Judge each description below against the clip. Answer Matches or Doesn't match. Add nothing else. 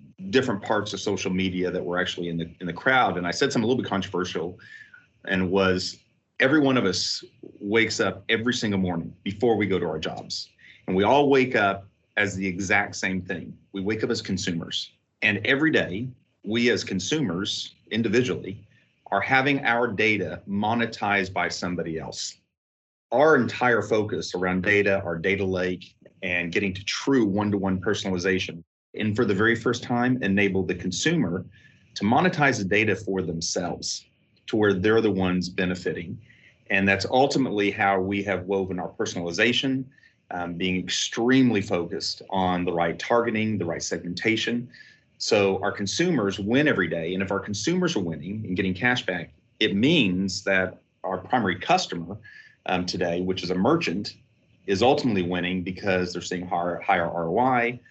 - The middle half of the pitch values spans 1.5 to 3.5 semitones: Matches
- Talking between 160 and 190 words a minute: Matches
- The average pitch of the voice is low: Matches